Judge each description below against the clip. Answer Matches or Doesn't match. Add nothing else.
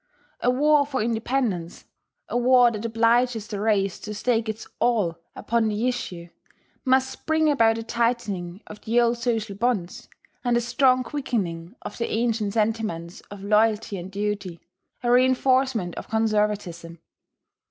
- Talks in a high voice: Matches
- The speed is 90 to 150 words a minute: Matches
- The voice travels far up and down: Doesn't match